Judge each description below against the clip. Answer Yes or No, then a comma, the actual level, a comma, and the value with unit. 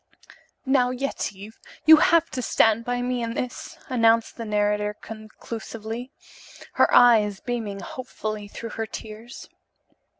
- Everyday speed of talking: No, slow, 125 wpm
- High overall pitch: Yes, high, 230 Hz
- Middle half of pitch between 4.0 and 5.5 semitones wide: No, narrow, 2.5 semitones